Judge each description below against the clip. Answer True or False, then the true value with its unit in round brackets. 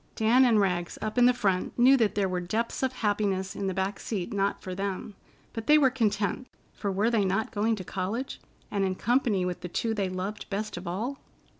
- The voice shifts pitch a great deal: False (3.4 semitones)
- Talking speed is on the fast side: True (215 wpm)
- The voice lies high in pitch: True (205 Hz)